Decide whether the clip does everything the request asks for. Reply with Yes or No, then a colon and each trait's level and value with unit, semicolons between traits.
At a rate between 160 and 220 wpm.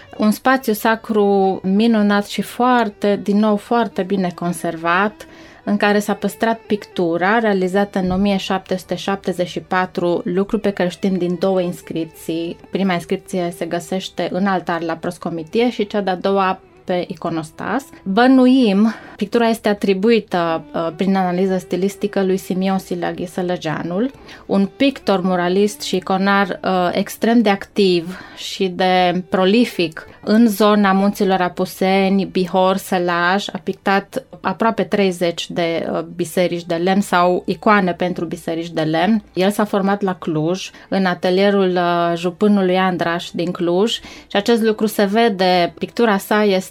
No: average, 135 wpm